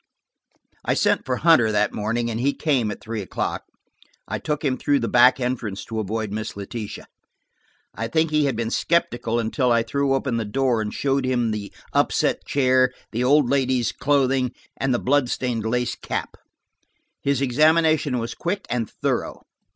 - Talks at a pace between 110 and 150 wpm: No, average, 175 wpm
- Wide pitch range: No, average, 3.4 semitones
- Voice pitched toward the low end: Yes, low, 125 Hz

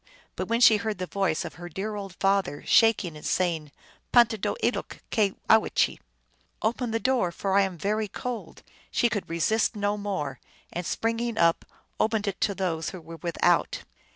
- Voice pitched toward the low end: No, high, 200 Hz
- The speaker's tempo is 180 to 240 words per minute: Yes, average, 185 wpm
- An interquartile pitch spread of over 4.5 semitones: No, average, 4.0 semitones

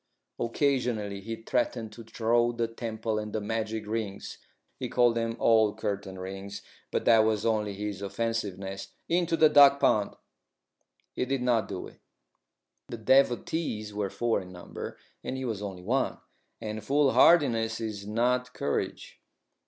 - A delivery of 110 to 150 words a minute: Yes, average, 145 wpm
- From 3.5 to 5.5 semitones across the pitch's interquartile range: No, average, 2.7 semitones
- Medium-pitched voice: No, low, 110 Hz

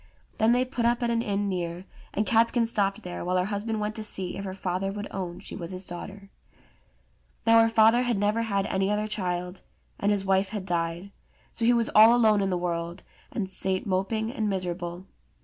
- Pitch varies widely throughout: No, average, 3.2 semitones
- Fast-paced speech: Yes, fast, 210 wpm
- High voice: Yes, high, 200 Hz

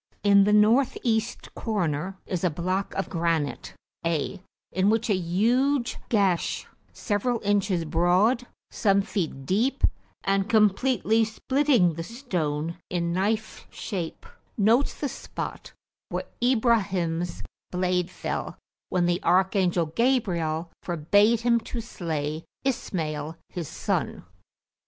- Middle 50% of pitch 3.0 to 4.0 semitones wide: No, average, 4.7 semitones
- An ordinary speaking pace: No, slow, 115 wpm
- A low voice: No, high, 195 Hz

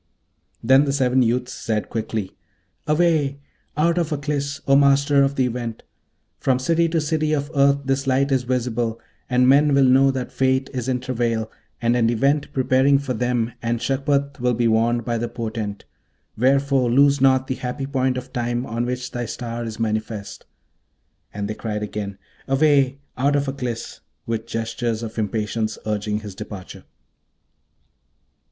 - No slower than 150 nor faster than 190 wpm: Yes, average, 160 wpm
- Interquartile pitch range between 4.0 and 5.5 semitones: No, average, 3.2 semitones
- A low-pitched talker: Yes, low, 125 Hz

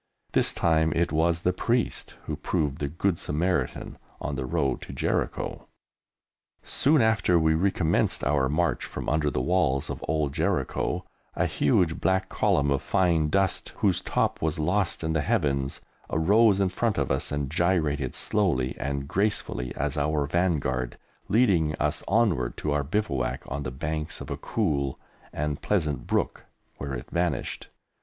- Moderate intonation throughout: Yes, average, 4.6 semitones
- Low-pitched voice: Yes, very low, 80 Hz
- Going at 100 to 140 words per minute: No, average, 160 wpm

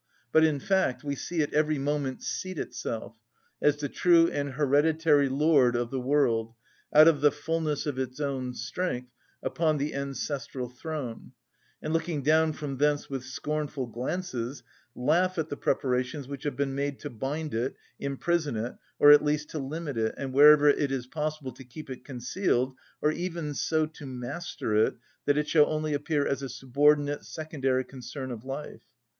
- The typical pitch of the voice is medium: Yes, medium, 145 Hz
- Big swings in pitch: No, average, 2.8 semitones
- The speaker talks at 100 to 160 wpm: No, average, 175 wpm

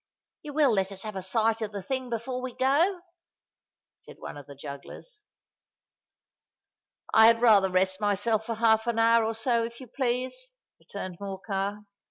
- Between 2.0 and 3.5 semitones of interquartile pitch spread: No, average, 4.0 semitones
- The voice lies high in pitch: Yes, high, 225 Hz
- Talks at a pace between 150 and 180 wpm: Yes, average, 170 wpm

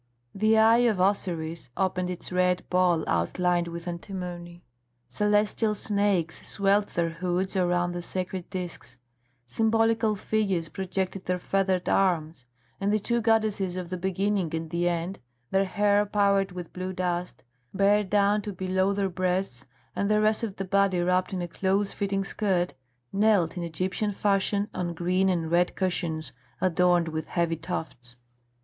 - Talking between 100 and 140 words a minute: No, average, 155 wpm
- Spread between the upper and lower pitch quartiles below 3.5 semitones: Yes, narrow, 2.4 semitones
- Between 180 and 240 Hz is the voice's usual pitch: Yes, medium, 185 Hz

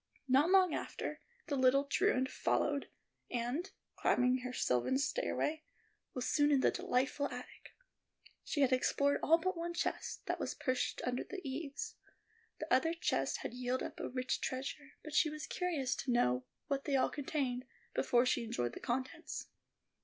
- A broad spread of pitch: No, average, 3.1 semitones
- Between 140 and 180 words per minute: Yes, average, 165 wpm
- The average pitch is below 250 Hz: No, very high, 270 Hz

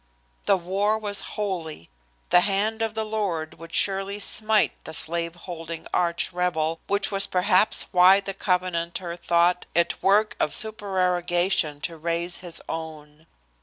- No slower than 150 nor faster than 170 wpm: No, average, 140 wpm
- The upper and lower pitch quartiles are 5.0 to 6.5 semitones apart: No, average, 3.0 semitones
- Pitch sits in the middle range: Yes, medium, 180 Hz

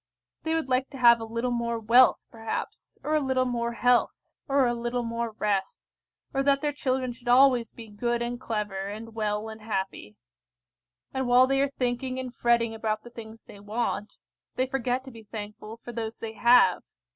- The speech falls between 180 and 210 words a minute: Yes, average, 190 wpm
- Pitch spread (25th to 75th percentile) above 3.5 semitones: No, narrow, 2.5 semitones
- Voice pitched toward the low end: No, high, 235 Hz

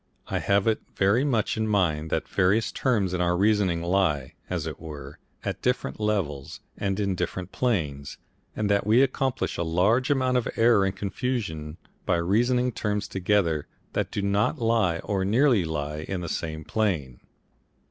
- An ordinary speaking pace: Yes, average, 170 wpm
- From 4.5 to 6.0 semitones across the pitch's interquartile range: Yes, average, 4.9 semitones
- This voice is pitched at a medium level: No, low, 100 Hz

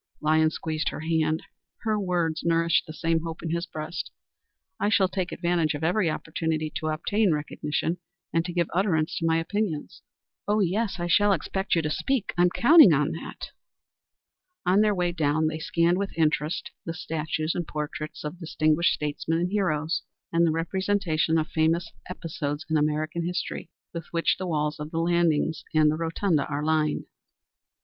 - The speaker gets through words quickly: No, average, 175 wpm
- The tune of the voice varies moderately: No, narrow, 2.3 semitones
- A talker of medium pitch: Yes, medium, 165 Hz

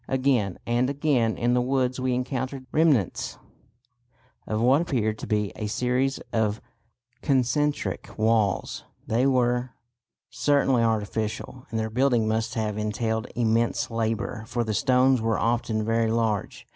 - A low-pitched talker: Yes, low, 120 Hz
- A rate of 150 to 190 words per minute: No, average, 140 wpm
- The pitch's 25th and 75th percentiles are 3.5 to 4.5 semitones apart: No, average, 2.7 semitones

